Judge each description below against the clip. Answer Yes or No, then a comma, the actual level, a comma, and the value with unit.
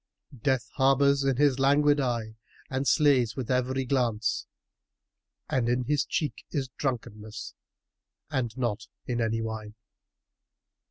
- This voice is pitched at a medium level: No, low, 130 Hz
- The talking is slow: Yes, slow, 125 wpm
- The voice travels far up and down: No, average, 3.2 semitones